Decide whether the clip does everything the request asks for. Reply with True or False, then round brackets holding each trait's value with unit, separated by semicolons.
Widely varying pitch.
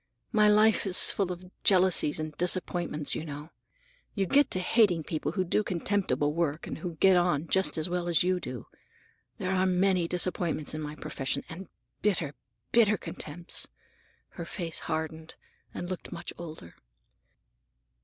False (3.0 semitones)